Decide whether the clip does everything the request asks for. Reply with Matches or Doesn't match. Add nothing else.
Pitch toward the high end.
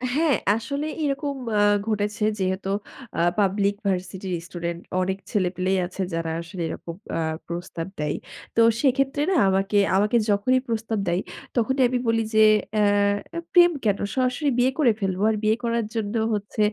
Matches